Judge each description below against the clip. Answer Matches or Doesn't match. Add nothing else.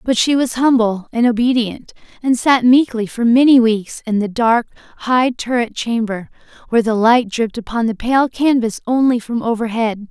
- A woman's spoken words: Matches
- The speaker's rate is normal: Matches